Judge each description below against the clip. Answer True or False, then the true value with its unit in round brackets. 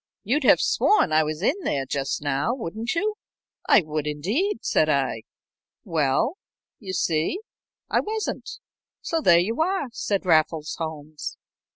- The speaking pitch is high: False (180 Hz)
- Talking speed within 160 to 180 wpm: False (145 wpm)